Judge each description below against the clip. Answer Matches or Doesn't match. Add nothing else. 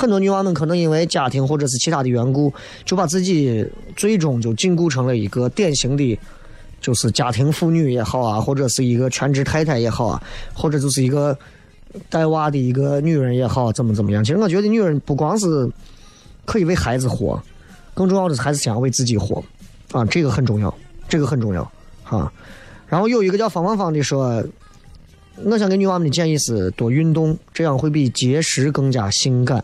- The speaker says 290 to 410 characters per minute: Matches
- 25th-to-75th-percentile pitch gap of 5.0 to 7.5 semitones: Matches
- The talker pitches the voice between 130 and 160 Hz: Matches